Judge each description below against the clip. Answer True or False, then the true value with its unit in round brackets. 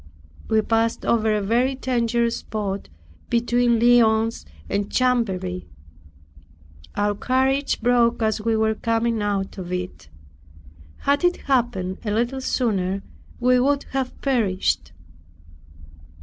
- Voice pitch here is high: True (230 Hz)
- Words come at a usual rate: False (115 wpm)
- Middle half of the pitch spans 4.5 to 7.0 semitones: False (3.1 semitones)